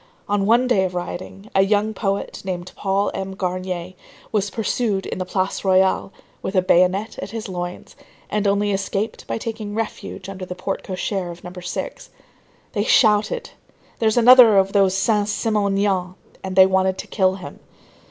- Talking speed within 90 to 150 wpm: No, average, 165 wpm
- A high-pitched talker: Yes, high, 195 Hz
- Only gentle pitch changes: Yes, narrow, 2.1 semitones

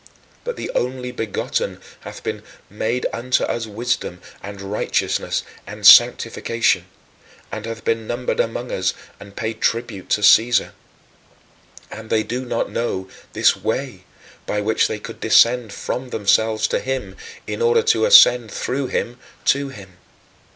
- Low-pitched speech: Yes, low, 115 Hz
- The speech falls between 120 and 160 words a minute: Yes, average, 145 wpm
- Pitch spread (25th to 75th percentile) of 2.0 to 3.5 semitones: Yes, average, 2.8 semitones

